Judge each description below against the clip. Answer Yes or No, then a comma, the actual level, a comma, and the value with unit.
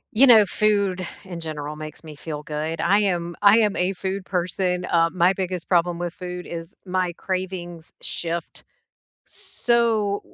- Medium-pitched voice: Yes, medium, 180 Hz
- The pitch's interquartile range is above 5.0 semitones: No, average, 2.8 semitones